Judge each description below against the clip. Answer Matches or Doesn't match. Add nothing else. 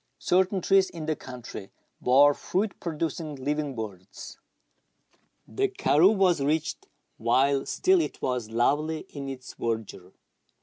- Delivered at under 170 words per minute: Matches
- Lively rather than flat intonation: Matches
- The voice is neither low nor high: Matches